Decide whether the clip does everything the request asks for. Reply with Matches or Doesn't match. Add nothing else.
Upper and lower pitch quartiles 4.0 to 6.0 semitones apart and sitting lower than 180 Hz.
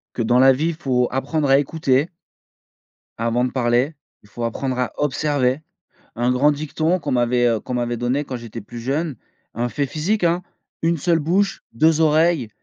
Matches